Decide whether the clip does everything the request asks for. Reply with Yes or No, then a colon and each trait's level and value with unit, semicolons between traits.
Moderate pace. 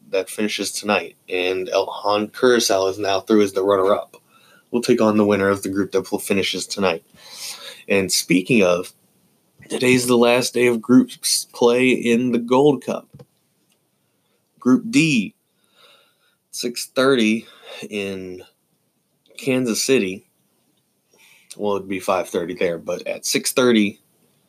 No: slow, 130 wpm